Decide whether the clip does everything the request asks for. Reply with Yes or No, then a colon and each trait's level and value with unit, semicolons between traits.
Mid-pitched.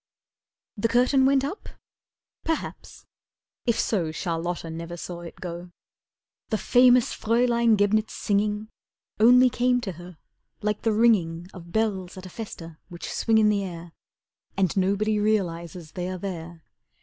No: high, 200 Hz